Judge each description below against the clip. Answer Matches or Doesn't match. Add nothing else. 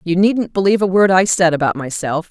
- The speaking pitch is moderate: Matches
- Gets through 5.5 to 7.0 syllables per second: Matches